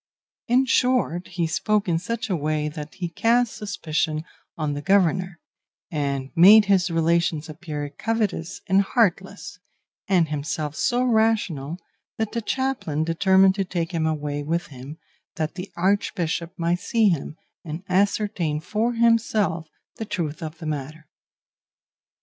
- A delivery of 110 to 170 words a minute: Yes, average, 140 wpm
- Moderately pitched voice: Yes, medium, 175 Hz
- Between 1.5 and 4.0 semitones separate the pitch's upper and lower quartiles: No, average, 4.8 semitones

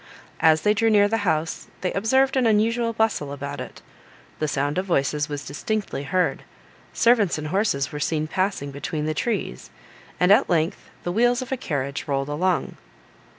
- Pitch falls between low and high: Yes, medium, 175 Hz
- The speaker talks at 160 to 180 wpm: Yes, average, 175 wpm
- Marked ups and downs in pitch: Yes, wide, 6.8 semitones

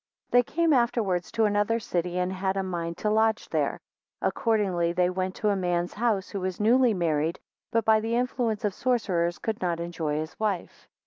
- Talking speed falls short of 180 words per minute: No, average, 195 wpm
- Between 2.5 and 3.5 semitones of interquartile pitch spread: No, average, 4.1 semitones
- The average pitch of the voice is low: No, high, 195 Hz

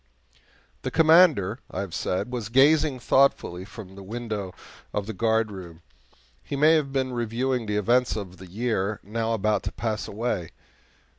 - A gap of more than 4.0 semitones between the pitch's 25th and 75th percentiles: Yes, average, 4.4 semitones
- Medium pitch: No, low, 110 Hz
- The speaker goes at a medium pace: Yes, average, 155 wpm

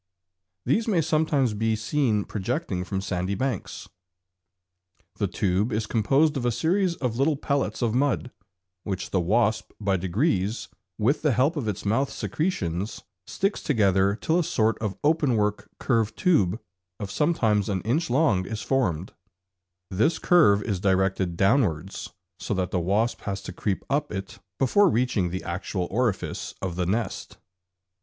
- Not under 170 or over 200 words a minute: No, average, 155 wpm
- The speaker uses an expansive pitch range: Yes, wide, 6.1 semitones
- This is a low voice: Yes, low, 110 Hz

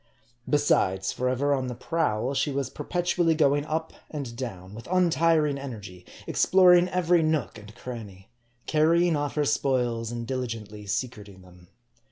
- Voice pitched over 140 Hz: No, low, 135 Hz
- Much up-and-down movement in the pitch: Yes, wide, 6.2 semitones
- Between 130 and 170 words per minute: Yes, average, 145 wpm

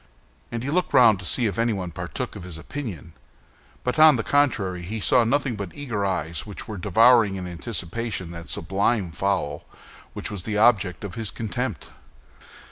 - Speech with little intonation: No, average, 4.7 semitones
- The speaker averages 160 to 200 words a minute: Yes, average, 175 wpm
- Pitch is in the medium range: No, low, 105 Hz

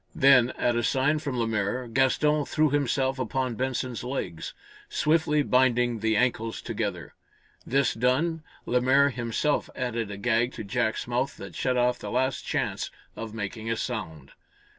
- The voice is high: No, low, 125 Hz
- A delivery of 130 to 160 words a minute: Yes, average, 150 wpm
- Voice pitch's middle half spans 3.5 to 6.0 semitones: No, average, 2.8 semitones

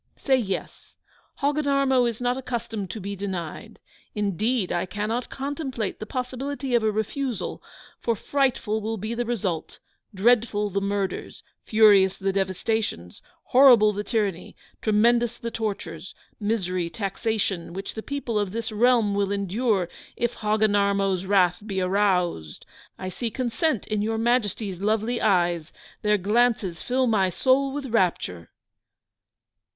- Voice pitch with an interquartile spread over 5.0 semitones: No, average, 3.7 semitones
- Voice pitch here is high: Yes, high, 215 Hz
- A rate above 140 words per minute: No, slow, 135 wpm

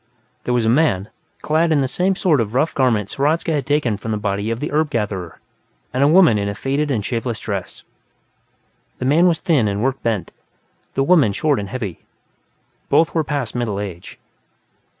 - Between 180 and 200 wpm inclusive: Yes, average, 190 wpm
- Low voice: Yes, low, 125 Hz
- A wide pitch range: Yes, wide, 6.3 semitones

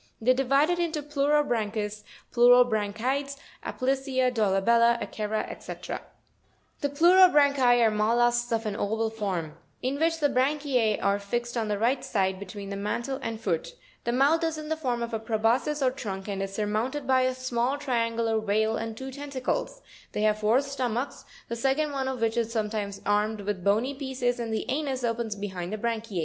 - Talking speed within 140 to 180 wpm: No, average, 190 wpm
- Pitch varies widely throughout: No, average, 4.0 semitones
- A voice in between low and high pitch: No, high, 235 Hz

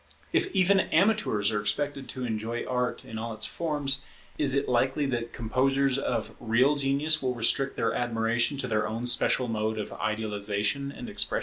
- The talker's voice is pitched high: No, low, 125 Hz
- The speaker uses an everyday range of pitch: Yes, average, 3.8 semitones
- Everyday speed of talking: Yes, average, 175 wpm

